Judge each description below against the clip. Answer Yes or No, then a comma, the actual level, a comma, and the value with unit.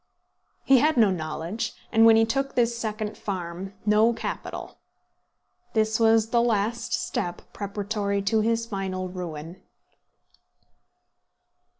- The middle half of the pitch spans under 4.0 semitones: Yes, average, 2.9 semitones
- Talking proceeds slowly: Yes, slow, 115 wpm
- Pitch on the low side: No, high, 215 Hz